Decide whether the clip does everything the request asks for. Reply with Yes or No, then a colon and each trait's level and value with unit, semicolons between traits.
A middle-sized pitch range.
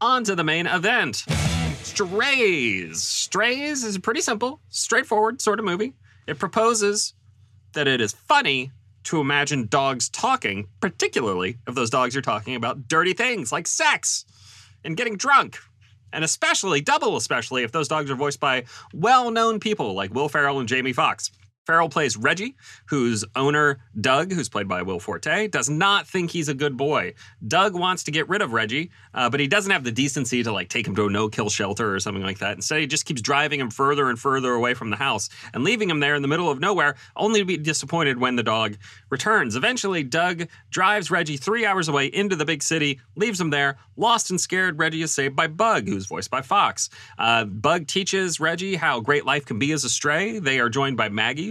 No: wide, 7.5 semitones